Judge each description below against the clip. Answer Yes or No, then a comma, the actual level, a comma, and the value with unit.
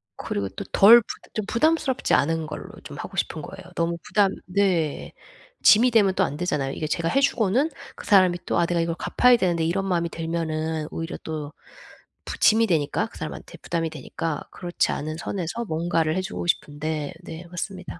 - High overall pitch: No, medium, 170 Hz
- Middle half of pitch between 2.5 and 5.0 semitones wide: Yes, average, 3.7 semitones